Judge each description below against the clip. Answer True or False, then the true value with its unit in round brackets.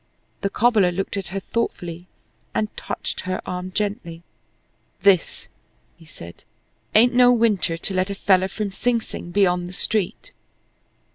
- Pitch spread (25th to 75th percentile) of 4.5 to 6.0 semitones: False (3.1 semitones)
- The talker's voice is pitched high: True (195 Hz)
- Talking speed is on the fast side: False (150 wpm)